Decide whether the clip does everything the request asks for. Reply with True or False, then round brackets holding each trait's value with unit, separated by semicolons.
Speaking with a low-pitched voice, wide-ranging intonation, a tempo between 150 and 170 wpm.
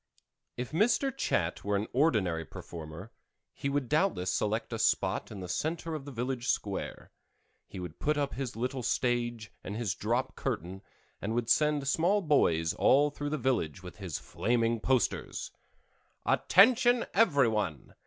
True (120 Hz; 6.5 semitones; 155 wpm)